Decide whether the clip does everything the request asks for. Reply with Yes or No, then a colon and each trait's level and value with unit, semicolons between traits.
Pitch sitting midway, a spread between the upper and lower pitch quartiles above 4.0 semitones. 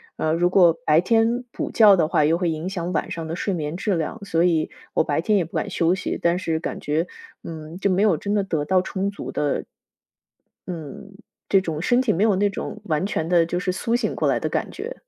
No: medium, 175 Hz; average, 3.7 semitones